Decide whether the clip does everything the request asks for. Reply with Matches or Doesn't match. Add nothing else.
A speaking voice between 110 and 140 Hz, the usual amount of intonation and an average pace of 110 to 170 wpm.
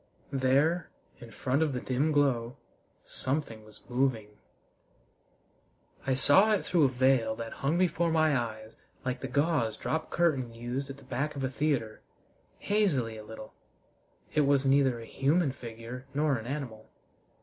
Matches